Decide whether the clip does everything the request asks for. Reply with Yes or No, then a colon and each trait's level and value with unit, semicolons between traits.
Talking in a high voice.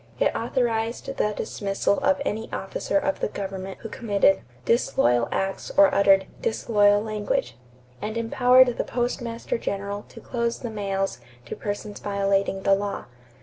Yes: high, 210 Hz